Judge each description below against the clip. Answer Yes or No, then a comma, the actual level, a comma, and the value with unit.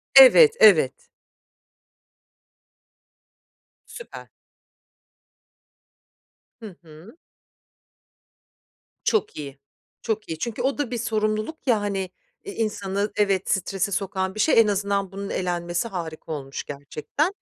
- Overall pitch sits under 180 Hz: No, high, 200 Hz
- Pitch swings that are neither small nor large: Yes, average, 4.3 semitones